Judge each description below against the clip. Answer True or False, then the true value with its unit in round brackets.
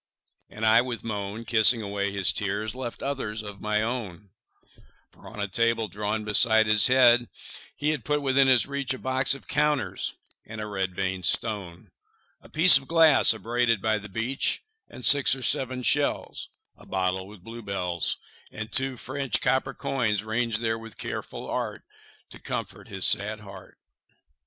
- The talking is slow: False (170 wpm)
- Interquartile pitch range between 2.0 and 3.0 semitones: False (3.9 semitones)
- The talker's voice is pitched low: True (110 Hz)